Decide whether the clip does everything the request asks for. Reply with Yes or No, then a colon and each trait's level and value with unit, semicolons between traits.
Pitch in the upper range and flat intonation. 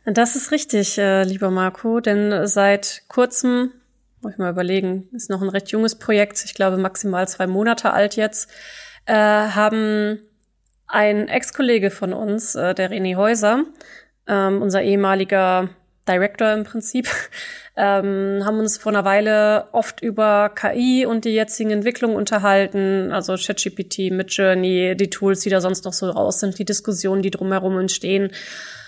Yes: high, 205 Hz; narrow, 2.2 semitones